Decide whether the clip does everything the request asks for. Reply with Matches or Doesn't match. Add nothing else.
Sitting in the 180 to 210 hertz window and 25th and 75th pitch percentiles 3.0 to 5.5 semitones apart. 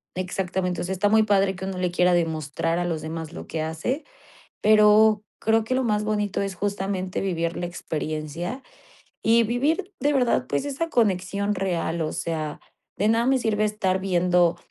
Matches